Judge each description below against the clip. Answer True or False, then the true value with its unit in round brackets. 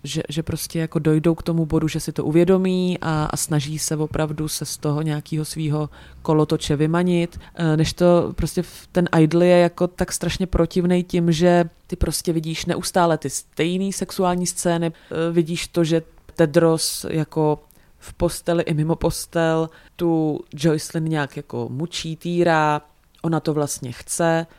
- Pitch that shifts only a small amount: True (1.9 semitones)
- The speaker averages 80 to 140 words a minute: False (155 wpm)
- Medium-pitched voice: True (165 Hz)